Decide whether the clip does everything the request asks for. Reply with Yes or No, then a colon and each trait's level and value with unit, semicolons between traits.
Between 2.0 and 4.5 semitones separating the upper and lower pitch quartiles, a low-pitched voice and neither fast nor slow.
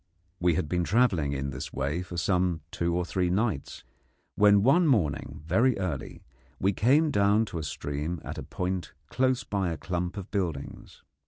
Yes: average, 4.1 semitones; very low, 90 Hz; average, 175 wpm